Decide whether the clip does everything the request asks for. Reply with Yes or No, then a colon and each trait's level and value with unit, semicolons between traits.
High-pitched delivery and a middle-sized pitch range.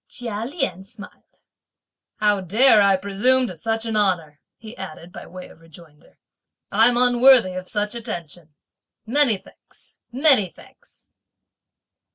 Yes: high, 210 Hz; average, 4.7 semitones